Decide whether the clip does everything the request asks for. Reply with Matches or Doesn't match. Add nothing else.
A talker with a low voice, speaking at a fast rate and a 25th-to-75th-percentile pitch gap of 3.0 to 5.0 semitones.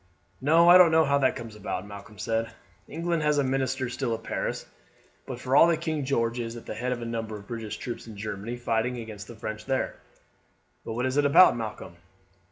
Matches